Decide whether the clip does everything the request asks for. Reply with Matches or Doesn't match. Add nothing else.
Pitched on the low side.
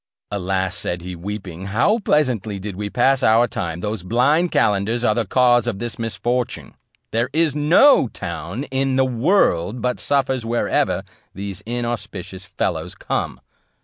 Matches